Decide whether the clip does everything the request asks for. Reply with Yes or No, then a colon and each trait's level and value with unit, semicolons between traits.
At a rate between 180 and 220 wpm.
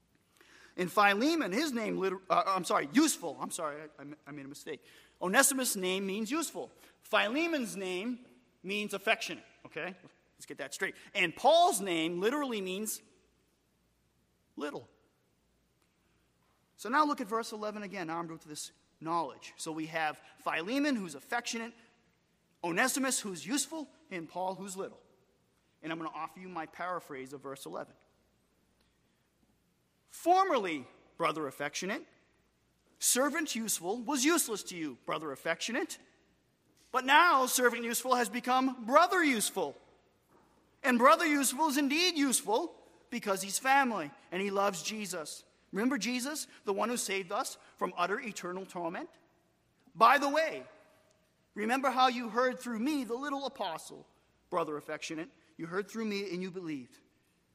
No: average, 140 wpm